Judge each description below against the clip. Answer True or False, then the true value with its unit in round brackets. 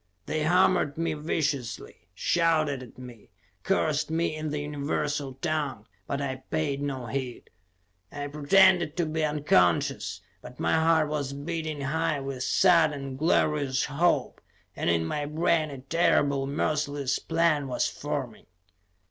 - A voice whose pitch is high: False (145 Hz)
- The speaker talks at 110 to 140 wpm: True (135 wpm)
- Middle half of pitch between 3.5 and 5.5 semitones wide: False (2.5 semitones)